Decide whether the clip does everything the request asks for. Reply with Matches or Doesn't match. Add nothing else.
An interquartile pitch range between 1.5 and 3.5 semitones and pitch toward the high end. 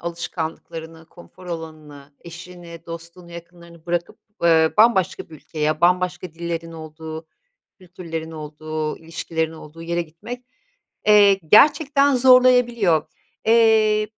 Doesn't match